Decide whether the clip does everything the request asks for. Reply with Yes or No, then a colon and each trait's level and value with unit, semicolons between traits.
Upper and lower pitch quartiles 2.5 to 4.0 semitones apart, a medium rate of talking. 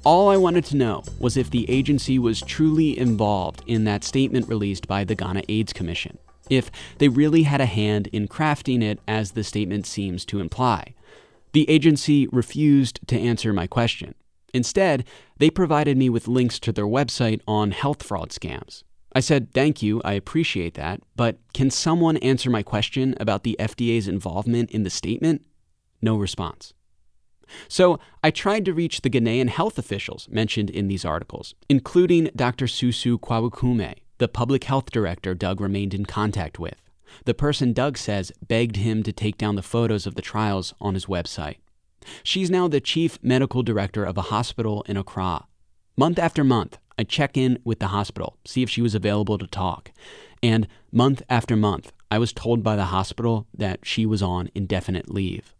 No: average, 4.6 semitones; average, 175 wpm